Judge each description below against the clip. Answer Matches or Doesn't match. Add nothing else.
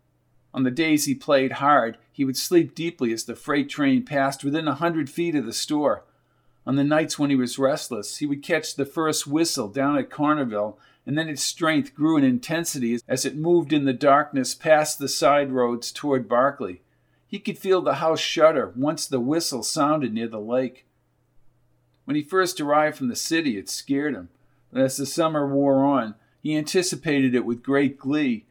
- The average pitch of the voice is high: Doesn't match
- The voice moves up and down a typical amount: Matches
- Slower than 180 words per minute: Doesn't match